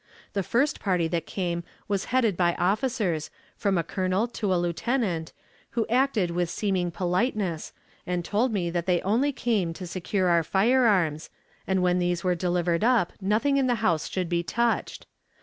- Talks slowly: No, average, 170 wpm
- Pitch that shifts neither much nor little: Yes, average, 4.3 semitones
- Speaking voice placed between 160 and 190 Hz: Yes, medium, 185 Hz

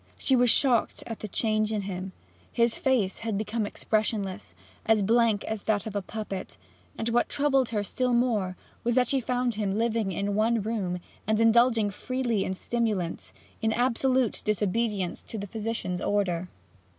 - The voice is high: Yes, high, 220 Hz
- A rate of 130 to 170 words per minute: Yes, average, 165 wpm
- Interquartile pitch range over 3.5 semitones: No, average, 2.7 semitones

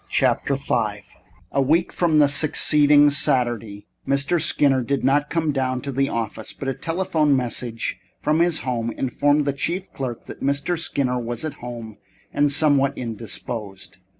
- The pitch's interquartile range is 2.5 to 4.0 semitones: Yes, average, 3.6 semitones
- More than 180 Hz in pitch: No, medium, 140 Hz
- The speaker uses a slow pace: No, average, 150 wpm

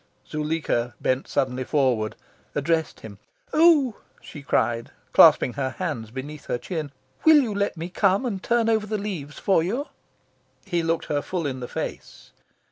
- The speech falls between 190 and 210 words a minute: No, average, 160 wpm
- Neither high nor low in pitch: Yes, medium, 160 Hz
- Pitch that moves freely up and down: Yes, wide, 7.4 semitones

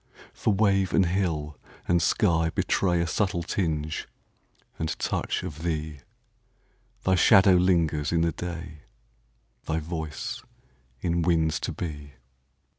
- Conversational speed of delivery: No, slow, 110 wpm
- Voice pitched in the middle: No, very low, 85 Hz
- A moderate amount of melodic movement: Yes, average, 3.2 semitones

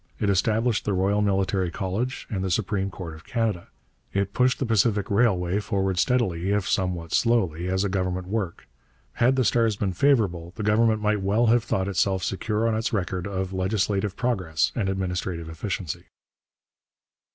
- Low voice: Yes, low, 100 Hz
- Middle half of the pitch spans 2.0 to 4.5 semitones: Yes, average, 3.0 semitones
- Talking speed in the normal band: Yes, average, 165 wpm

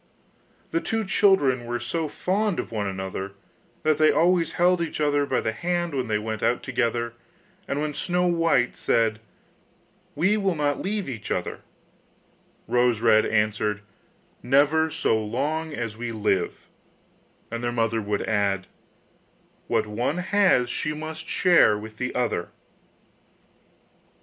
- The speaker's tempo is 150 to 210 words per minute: No, average, 140 wpm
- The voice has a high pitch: No, low, 125 Hz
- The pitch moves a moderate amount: No, wide, 6.9 semitones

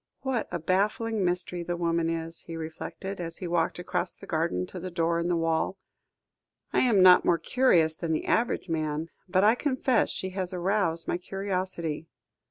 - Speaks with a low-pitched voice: No, medium, 175 Hz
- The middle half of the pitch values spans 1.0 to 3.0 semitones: Yes, average, 2.7 semitones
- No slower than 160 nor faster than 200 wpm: Yes, average, 180 wpm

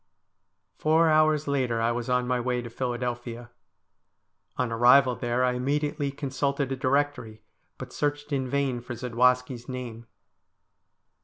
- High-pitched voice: No, low, 125 Hz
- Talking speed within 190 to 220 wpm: No, average, 140 wpm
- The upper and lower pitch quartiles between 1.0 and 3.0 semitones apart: Yes, narrow, 2.5 semitones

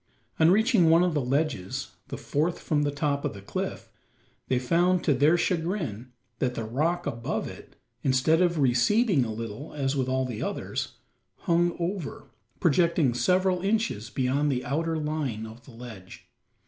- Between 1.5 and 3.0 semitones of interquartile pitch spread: No, wide, 5.5 semitones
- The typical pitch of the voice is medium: Yes, medium, 145 Hz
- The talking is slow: No, average, 165 wpm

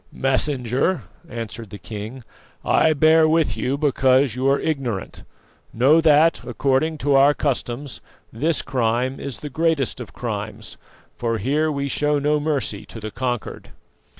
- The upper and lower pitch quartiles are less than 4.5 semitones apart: Yes, average, 3.6 semitones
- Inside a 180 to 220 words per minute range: No, average, 145 wpm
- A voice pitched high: No, low, 135 Hz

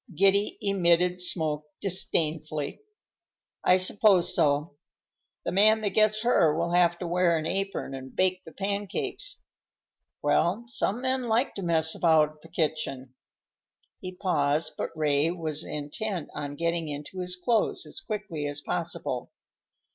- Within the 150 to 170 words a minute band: No, average, 140 wpm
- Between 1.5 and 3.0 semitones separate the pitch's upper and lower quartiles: No, average, 4.2 semitones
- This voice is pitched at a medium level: Yes, medium, 175 Hz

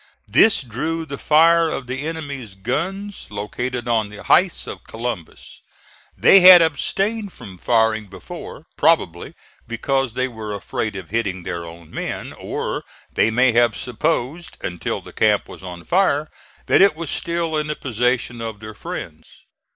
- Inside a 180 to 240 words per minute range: No, average, 155 wpm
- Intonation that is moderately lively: No, wide, 6.8 semitones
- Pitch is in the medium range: No, low, 125 Hz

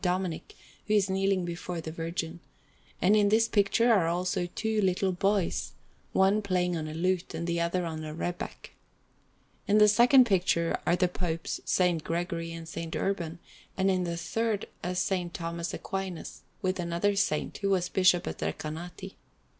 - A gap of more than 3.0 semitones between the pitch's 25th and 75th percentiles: No, narrow, 2.6 semitones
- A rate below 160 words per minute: No, average, 170 wpm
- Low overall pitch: No, medium, 180 Hz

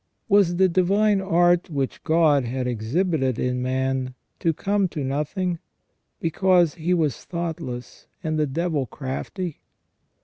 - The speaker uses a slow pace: Yes, slow, 130 wpm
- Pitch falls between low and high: Yes, medium, 160 Hz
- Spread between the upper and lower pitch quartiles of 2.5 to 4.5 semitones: No, average, 5.2 semitones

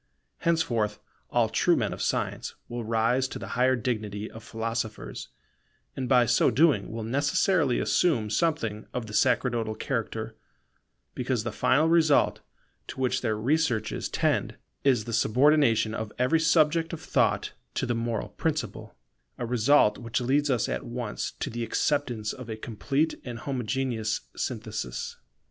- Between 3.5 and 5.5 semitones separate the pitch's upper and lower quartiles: Yes, average, 4.2 semitones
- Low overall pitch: Yes, low, 120 Hz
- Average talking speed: Yes, average, 150 wpm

